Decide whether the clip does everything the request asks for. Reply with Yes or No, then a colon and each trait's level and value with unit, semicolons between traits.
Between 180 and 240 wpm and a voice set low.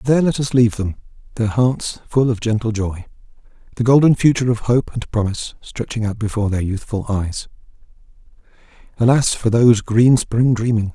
No: average, 165 wpm; low, 115 Hz